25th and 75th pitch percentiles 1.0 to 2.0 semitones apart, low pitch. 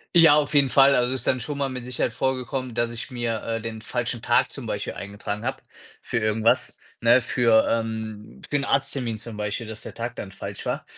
No: average, 2.7 semitones; low, 120 Hz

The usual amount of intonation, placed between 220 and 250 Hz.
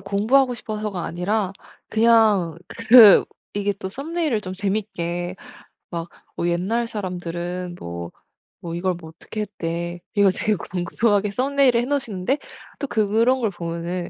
No: average, 4.4 semitones; high, 200 Hz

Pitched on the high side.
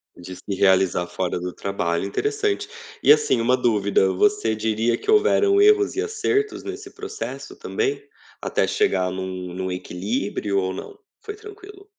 No: low, 120 Hz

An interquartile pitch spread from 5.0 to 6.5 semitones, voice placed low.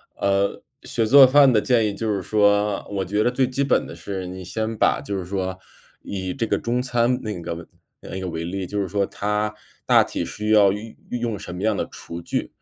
No: average, 3.2 semitones; low, 105 Hz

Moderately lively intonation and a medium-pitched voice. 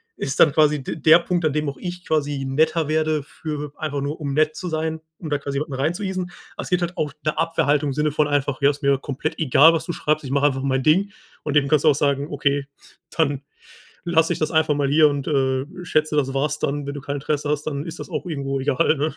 No: narrow, 2.0 semitones; medium, 150 Hz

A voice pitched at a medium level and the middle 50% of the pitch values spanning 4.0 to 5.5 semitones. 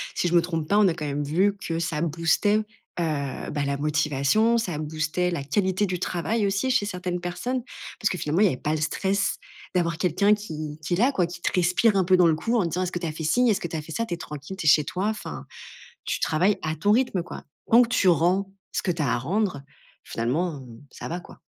Yes: medium, 175 Hz; average, 4.3 semitones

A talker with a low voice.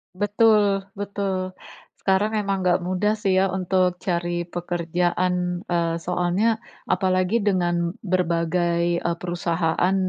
No: medium, 180 Hz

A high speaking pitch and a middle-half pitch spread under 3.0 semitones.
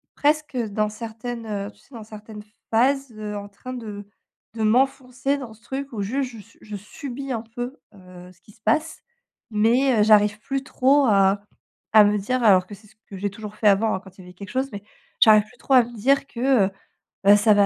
No: high, 220 Hz; average, 3.7 semitones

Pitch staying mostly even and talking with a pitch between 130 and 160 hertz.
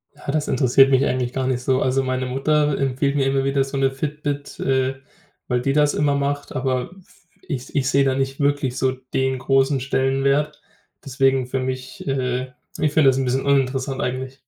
Yes: narrow, 1.3 semitones; low, 135 Hz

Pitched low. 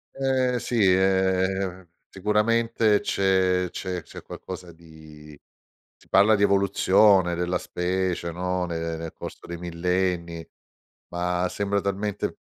Yes: very low, 95 Hz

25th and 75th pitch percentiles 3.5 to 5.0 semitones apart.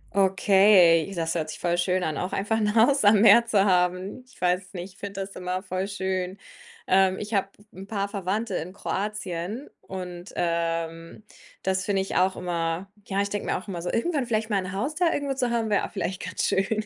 No: narrow, 2.6 semitones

